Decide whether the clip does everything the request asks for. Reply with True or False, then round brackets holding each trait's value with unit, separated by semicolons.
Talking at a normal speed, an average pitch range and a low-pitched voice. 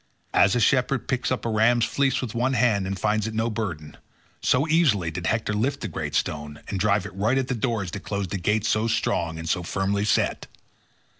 False (220 wpm; 3.8 semitones; 110 Hz)